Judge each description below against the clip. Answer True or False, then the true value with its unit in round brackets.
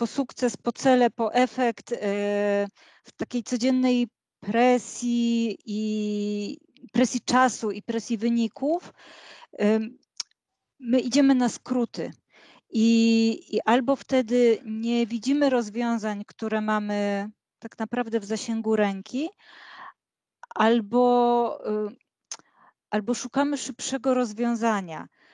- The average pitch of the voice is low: False (235 Hz)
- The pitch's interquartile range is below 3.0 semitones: True (2.5 semitones)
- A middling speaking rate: False (90 wpm)